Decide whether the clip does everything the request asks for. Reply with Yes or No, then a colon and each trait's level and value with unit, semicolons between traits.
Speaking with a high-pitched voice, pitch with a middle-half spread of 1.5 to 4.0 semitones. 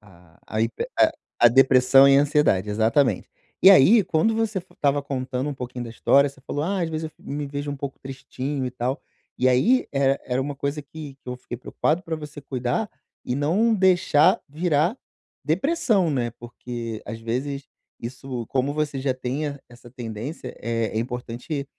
No: medium, 140 Hz; average, 3.5 semitones